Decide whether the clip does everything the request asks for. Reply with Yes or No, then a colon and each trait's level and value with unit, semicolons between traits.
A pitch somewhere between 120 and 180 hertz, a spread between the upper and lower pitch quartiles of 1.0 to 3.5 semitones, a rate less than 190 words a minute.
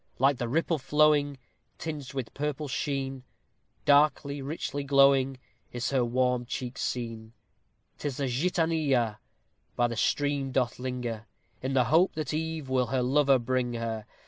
Yes: low, 135 Hz; average, 2.8 semitones; average, 145 wpm